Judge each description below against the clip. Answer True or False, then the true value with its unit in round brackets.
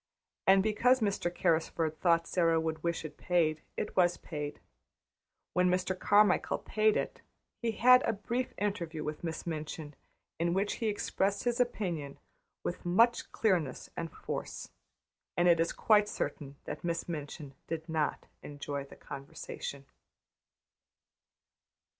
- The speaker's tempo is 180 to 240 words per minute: False (135 wpm)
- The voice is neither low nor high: True (175 Hz)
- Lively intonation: False (4.5 semitones)